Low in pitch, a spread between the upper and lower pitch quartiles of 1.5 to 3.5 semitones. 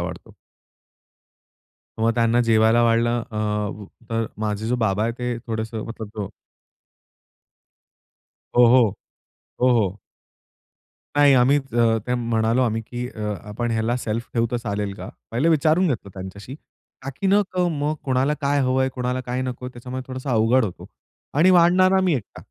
Yes: low, 120 Hz; average, 2.8 semitones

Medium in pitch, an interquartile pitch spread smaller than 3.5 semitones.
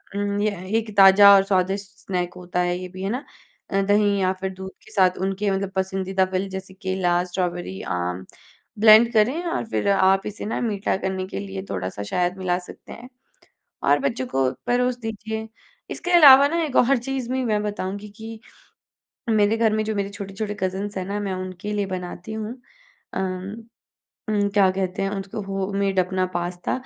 No: high, 195 Hz; narrow, 2.4 semitones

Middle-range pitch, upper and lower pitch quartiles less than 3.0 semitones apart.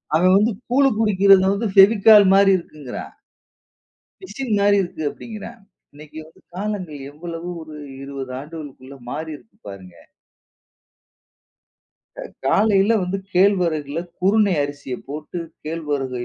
No: medium, 175 Hz; wide, 5.4 semitones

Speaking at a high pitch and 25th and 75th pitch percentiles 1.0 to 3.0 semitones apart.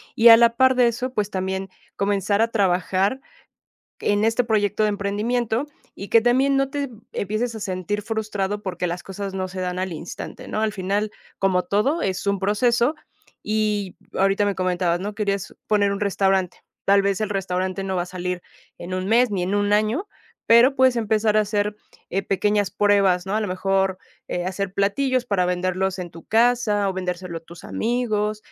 Yes: high, 200 Hz; average, 2.7 semitones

